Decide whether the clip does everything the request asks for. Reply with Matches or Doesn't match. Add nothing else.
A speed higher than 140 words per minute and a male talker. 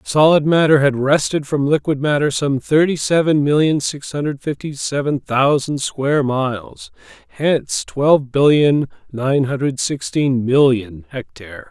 Doesn't match